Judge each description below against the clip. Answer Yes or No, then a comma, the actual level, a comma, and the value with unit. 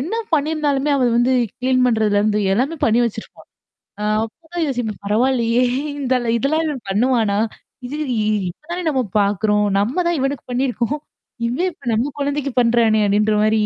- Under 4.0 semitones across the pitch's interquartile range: No, average, 4.5 semitones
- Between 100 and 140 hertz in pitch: No, high, 245 Hz